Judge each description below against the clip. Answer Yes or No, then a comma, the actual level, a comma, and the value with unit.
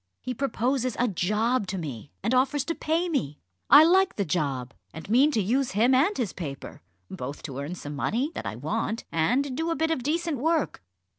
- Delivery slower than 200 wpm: No, fast, 205 wpm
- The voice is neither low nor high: No, high, 240 Hz